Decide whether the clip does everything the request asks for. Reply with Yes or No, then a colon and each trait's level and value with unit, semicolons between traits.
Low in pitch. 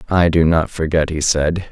Yes: very low, 80 Hz